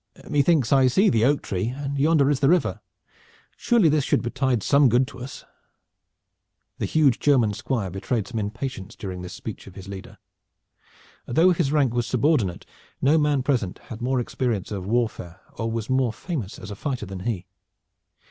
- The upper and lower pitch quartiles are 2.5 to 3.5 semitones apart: No, average, 5.1 semitones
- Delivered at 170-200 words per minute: Yes, average, 175 wpm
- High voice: No, low, 125 Hz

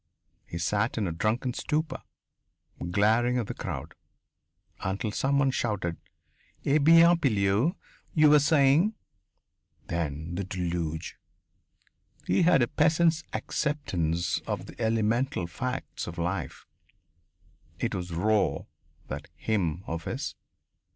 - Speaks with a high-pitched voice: No, low, 110 Hz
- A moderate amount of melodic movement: No, wide, 8.4 semitones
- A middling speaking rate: No, slow, 115 wpm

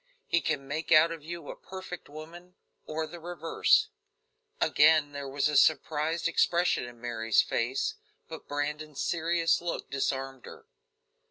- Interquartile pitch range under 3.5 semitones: Yes, average, 3.0 semitones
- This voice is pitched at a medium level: Yes, medium, 155 Hz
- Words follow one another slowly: No, average, 145 wpm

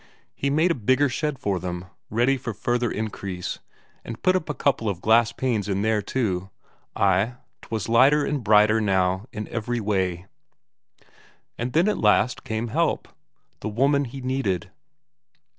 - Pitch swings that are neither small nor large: Yes, average, 4.5 semitones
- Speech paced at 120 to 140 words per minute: No, average, 155 wpm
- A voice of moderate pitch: No, low, 115 Hz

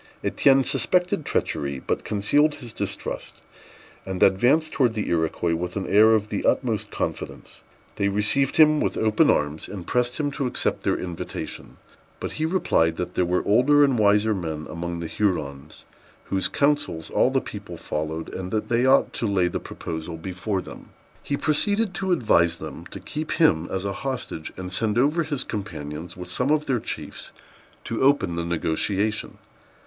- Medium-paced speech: Yes, average, 175 wpm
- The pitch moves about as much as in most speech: No, wide, 7.9 semitones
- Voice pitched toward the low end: Yes, low, 105 Hz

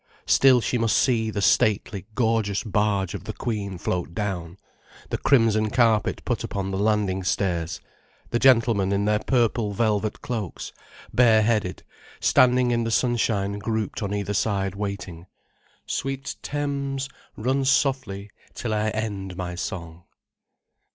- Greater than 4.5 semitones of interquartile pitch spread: No, average, 3.2 semitones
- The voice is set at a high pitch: No, low, 105 Hz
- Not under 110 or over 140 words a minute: Yes, slow, 135 wpm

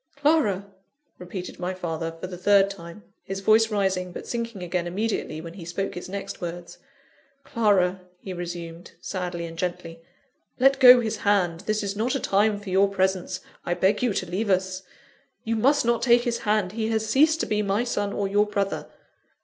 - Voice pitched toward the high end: Yes, high, 195 Hz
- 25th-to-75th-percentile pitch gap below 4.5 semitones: Yes, average, 3.4 semitones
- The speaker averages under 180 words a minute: No, average, 190 wpm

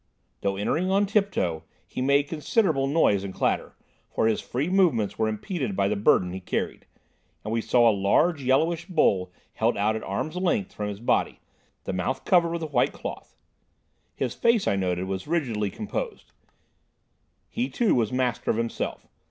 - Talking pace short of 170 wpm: No, average, 175 wpm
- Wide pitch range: Yes, wide, 8.9 semitones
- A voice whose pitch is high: No, low, 125 Hz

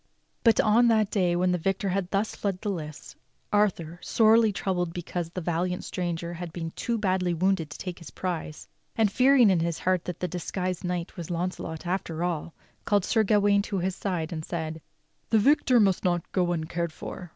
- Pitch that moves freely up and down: No, average, 2.9 semitones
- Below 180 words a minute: No, average, 195 wpm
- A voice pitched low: No, medium, 180 Hz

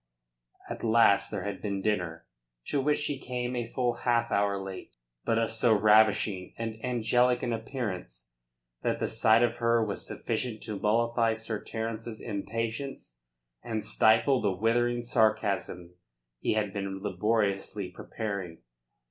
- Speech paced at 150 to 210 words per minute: No, average, 140 wpm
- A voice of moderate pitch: No, low, 110 Hz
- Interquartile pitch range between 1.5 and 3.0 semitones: Yes, average, 2.7 semitones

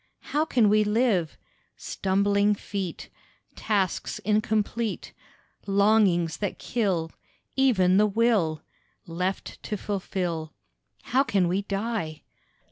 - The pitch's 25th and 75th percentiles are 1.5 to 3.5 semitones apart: Yes, average, 3.0 semitones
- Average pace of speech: No, slow, 100 wpm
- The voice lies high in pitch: Yes, high, 200 Hz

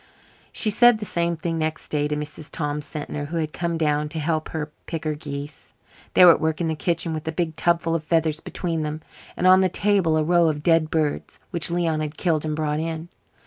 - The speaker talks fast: Yes, fast, 230 wpm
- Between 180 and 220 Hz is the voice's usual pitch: No, medium, 160 Hz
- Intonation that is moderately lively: No, narrow, 1.9 semitones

